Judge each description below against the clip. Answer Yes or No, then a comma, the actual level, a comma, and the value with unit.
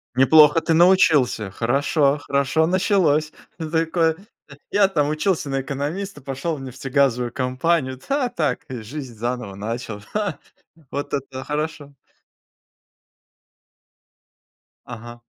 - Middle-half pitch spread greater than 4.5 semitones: No, average, 4.0 semitones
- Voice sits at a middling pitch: Yes, medium, 145 Hz